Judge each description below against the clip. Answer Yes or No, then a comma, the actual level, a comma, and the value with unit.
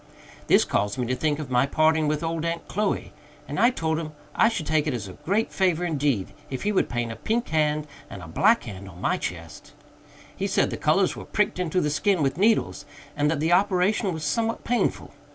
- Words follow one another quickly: Yes, fast, 225 wpm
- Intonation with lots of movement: Yes, wide, 6.1 semitones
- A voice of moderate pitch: Yes, medium, 155 Hz